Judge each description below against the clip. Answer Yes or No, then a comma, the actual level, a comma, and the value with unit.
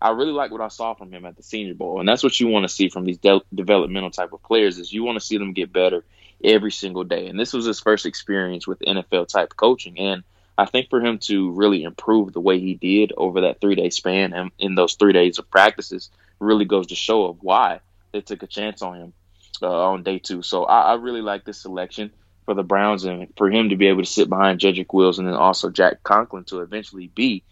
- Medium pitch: No, very low, 95 Hz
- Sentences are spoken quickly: Yes, fast, 255 wpm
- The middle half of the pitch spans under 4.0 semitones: Yes, narrow, 2.4 semitones